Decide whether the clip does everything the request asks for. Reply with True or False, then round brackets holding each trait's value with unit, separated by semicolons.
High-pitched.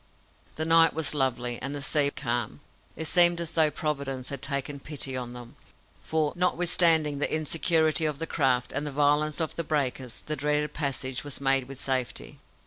False (145 Hz)